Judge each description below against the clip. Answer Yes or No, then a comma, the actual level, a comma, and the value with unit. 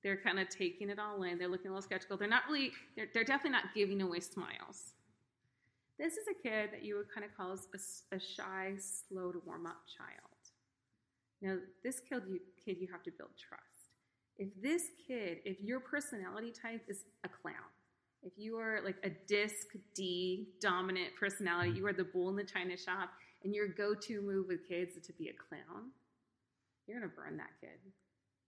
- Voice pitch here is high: Yes, high, 195 Hz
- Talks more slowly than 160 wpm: No, average, 195 wpm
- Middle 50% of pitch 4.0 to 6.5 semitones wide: No, narrow, 2.6 semitones